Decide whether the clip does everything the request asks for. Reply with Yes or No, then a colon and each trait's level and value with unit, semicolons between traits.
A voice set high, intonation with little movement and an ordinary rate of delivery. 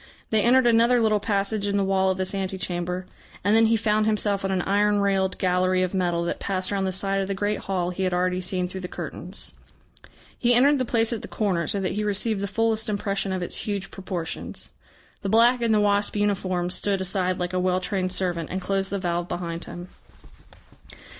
No: high, 195 Hz; narrow, 2.2 semitones; fast, 220 wpm